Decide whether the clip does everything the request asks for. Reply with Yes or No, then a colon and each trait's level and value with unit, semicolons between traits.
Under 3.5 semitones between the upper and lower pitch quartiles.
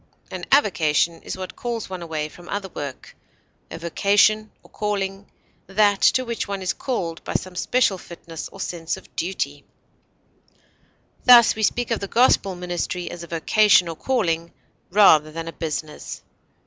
No: average, 4.0 semitones